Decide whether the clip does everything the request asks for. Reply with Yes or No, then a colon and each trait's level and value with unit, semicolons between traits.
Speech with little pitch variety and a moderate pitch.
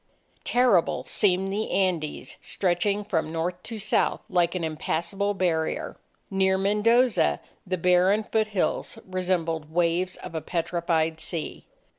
No: average, 3.2 semitones; medium, 180 Hz